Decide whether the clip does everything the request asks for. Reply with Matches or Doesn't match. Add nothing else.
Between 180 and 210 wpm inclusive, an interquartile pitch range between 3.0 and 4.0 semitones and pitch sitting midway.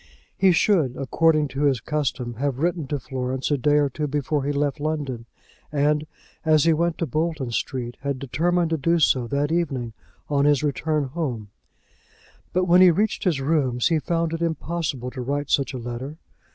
Matches